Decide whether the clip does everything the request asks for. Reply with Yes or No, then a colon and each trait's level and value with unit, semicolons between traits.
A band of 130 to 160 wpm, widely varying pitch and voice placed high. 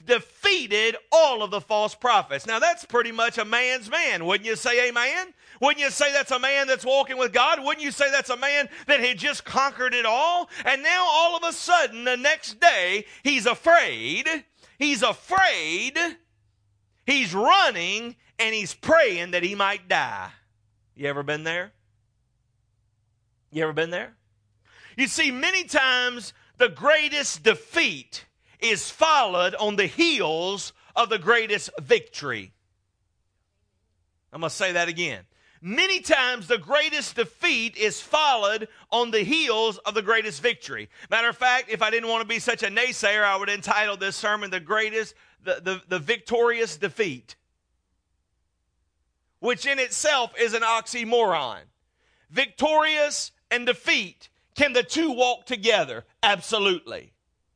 Yes: average, 150 wpm; wide, 7.9 semitones; high, 230 Hz